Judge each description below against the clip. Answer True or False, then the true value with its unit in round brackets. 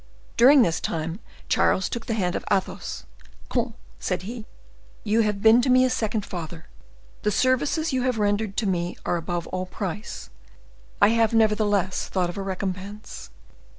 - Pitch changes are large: False (3.7 semitones)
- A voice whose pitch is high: True (205 Hz)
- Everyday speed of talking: True (165 wpm)